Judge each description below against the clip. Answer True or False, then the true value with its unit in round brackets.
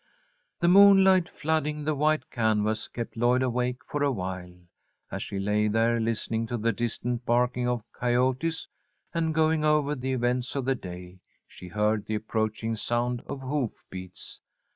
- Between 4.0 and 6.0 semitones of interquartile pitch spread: True (4.7 semitones)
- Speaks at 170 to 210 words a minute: False (155 wpm)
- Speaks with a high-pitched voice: False (120 Hz)